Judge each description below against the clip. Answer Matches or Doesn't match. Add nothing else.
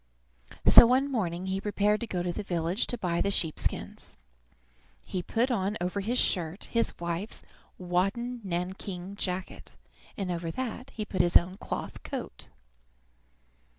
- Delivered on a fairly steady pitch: Doesn't match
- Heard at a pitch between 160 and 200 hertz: Matches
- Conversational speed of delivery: Matches